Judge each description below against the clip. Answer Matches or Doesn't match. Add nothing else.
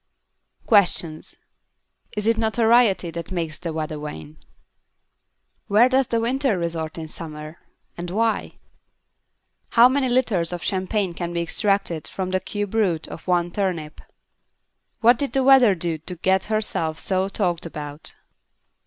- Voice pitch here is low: Doesn't match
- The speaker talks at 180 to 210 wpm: Doesn't match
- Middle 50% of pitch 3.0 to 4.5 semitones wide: Doesn't match